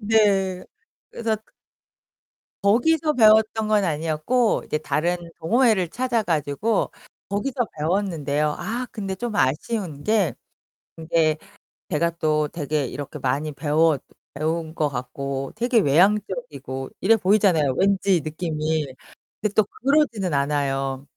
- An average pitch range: No, wide, 6.2 semitones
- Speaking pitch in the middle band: Yes, medium, 170 Hz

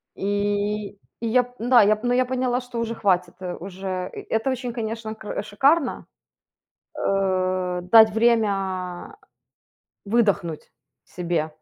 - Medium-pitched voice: No, high, 205 Hz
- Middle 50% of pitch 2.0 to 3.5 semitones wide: No, average, 4.0 semitones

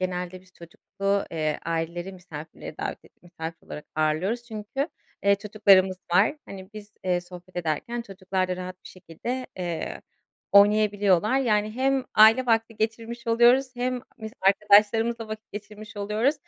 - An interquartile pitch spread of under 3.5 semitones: No, average, 3.8 semitones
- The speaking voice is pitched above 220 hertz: No, high, 205 Hz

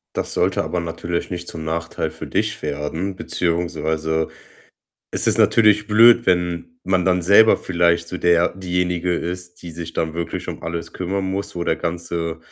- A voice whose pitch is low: Yes, very low, 85 Hz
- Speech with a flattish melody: Yes, narrow, 1.8 semitones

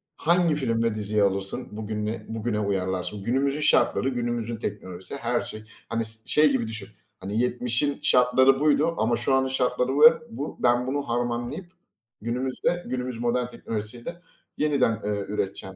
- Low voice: Yes, low, 120 Hz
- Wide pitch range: No, average, 3.7 semitones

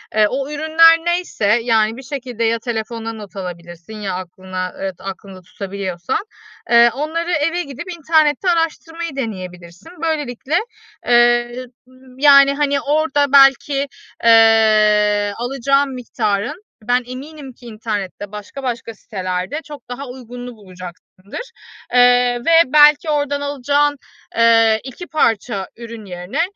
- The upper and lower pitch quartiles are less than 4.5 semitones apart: No, wide, 5.5 semitones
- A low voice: No, high, 245 Hz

